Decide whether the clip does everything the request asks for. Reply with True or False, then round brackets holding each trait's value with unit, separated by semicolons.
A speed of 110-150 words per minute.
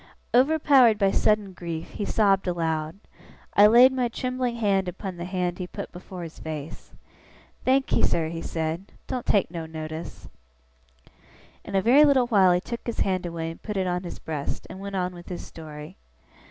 False (180 wpm)